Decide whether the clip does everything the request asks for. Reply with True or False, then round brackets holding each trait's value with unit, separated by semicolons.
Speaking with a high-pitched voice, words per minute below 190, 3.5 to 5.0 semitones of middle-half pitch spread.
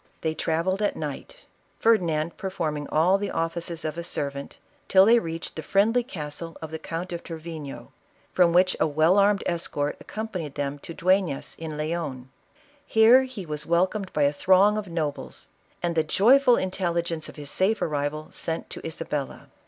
False (170 Hz; 175 wpm; 3.8 semitones)